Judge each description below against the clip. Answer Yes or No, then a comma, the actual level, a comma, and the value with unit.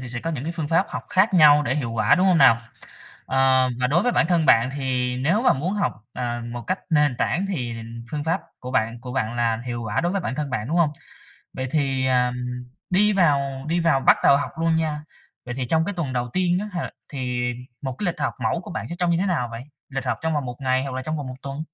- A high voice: No, medium, 140 Hz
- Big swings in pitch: No, average, 4.9 semitones